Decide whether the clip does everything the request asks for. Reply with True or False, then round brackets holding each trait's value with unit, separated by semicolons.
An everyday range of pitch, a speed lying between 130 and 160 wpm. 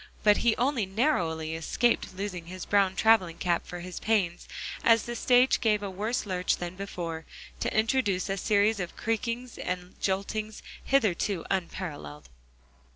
True (3.9 semitones; 150 wpm)